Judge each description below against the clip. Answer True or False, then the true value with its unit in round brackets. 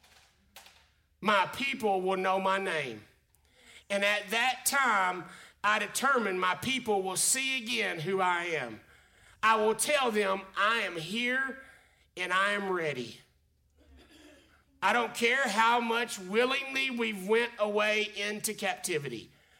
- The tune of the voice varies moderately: True (4.3 semitones)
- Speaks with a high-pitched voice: True (205 Hz)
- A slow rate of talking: True (130 wpm)